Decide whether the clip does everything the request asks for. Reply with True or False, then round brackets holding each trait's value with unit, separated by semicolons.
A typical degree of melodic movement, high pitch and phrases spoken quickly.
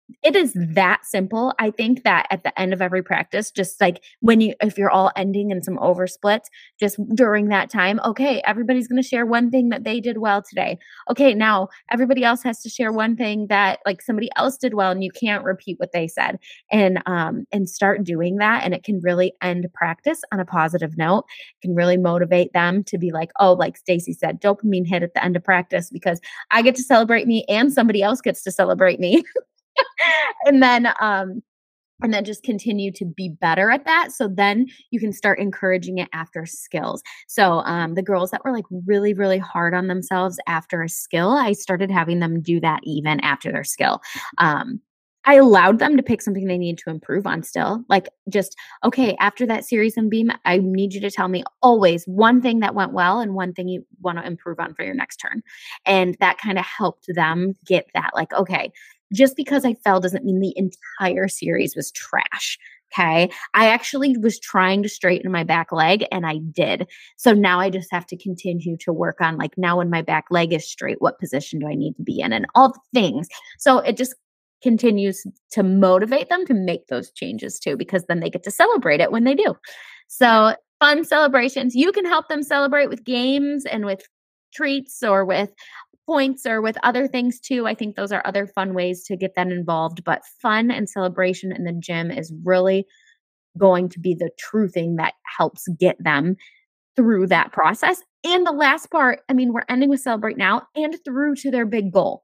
True (5.0 semitones; 200 Hz; 210 wpm)